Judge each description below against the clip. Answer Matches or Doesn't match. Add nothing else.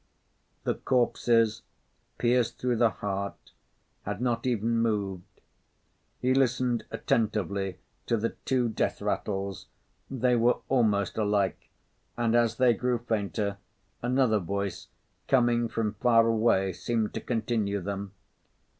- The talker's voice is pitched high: Doesn't match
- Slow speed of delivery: Matches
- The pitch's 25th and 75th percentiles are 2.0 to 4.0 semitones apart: Matches